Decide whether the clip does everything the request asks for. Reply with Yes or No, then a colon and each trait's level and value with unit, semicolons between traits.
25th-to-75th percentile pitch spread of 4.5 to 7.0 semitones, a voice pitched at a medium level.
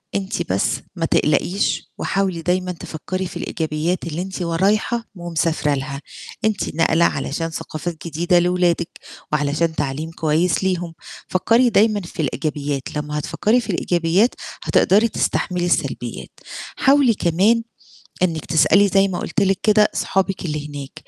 No: average, 3.7 semitones; medium, 175 Hz